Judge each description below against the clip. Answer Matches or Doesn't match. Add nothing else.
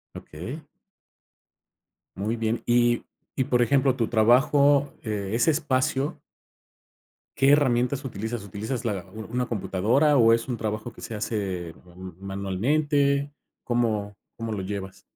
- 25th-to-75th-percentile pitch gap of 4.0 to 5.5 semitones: Matches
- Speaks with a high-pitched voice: Doesn't match